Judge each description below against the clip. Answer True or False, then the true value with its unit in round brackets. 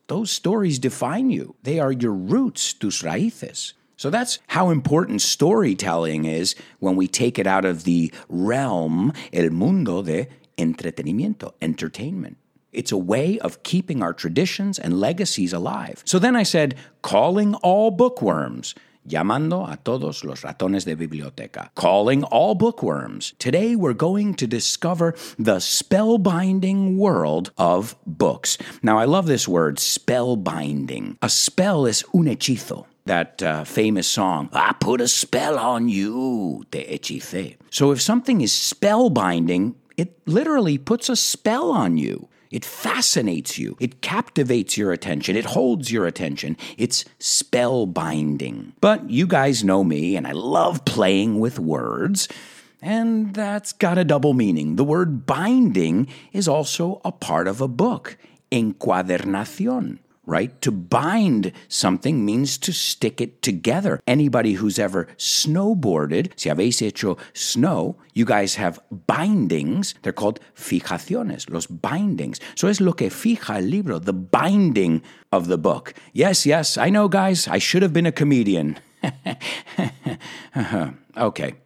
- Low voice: False (145 Hz)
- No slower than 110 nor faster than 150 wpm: True (140 wpm)